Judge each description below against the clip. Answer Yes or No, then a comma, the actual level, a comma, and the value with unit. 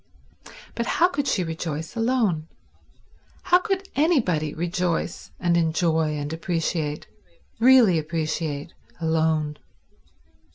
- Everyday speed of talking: No, slow, 95 wpm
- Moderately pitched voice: Yes, medium, 165 Hz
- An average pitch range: No, wide, 6.4 semitones